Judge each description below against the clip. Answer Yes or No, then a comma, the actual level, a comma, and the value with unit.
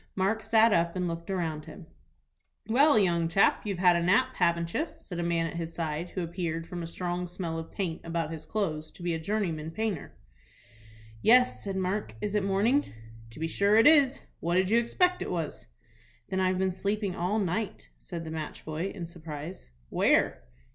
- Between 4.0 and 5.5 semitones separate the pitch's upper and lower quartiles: No, average, 3.6 semitones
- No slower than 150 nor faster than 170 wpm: No, average, 195 wpm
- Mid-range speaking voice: Yes, medium, 180 Hz